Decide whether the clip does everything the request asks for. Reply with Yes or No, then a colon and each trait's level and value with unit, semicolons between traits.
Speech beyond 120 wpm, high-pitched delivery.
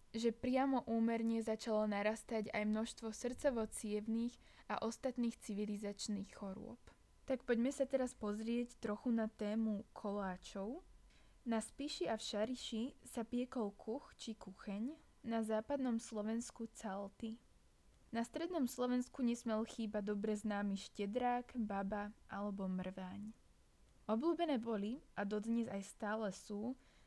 No: average, 115 wpm; high, 225 Hz